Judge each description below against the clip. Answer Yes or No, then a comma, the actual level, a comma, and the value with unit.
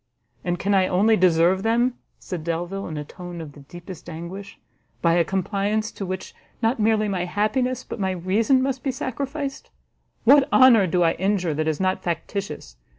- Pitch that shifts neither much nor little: Yes, average, 4.3 semitones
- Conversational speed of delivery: Yes, average, 180 wpm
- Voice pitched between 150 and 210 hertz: Yes, high, 190 Hz